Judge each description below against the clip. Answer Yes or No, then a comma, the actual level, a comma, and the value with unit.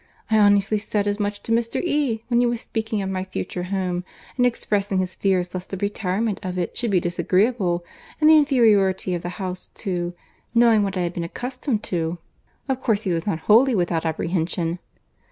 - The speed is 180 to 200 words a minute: Yes, average, 190 wpm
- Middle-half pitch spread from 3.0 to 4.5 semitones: Yes, average, 3.9 semitones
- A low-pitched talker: No, high, 195 Hz